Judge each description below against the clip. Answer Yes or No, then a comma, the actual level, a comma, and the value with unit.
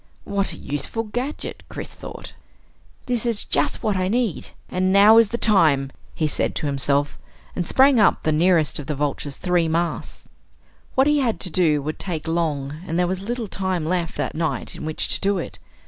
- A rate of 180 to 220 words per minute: Yes, average, 195 wpm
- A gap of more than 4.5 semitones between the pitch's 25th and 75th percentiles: Yes, average, 5.3 semitones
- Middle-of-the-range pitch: Yes, medium, 180 Hz